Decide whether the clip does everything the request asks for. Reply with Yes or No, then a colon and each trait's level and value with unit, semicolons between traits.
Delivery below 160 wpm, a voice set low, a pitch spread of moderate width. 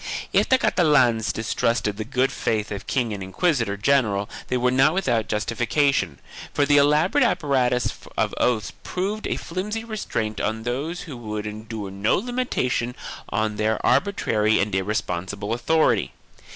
No: average, 150 wpm; low, 120 Hz; wide, 5.8 semitones